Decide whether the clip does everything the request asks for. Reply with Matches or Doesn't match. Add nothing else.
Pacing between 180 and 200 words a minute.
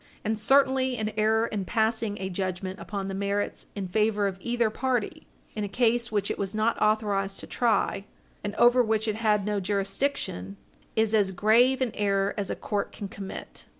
Matches